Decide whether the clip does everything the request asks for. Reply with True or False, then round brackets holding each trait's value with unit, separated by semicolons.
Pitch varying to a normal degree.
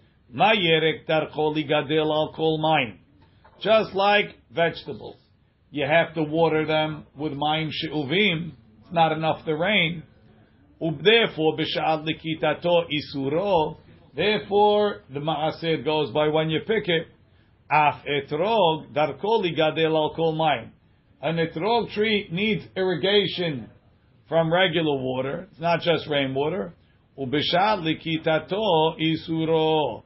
False (2.1 semitones)